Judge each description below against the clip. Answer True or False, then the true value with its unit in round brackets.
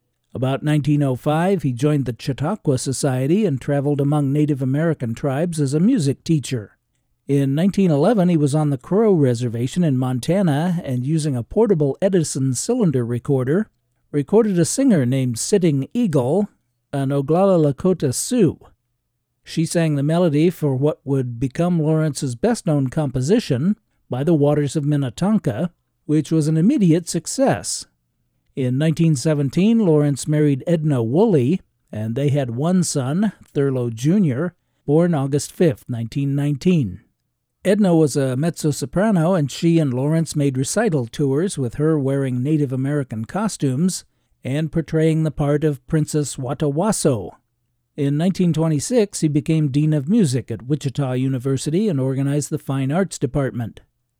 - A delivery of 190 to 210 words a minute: False (135 wpm)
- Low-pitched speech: False (150 Hz)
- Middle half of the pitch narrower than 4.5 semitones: True (3.8 semitones)